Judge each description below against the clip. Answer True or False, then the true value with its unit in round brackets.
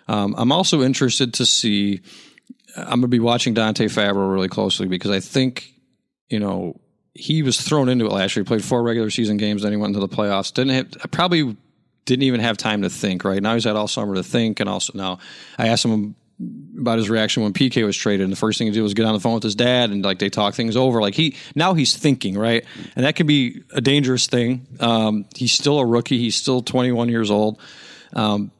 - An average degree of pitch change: True (3.8 semitones)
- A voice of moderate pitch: False (115 Hz)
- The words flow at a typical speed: False (235 wpm)